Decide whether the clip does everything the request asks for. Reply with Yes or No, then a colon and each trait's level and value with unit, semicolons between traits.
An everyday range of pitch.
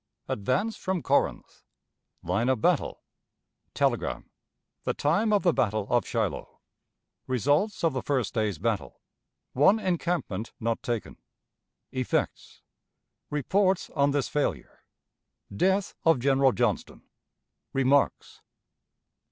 No: wide, 6.7 semitones